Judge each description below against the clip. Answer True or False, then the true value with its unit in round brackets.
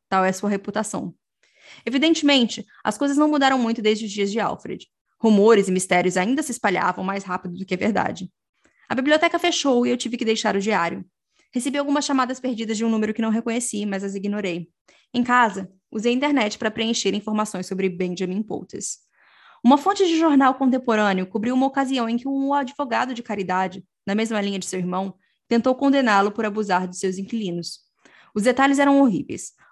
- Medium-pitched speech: False (225 Hz)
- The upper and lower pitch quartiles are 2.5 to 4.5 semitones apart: False (5.2 semitones)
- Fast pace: True (190 wpm)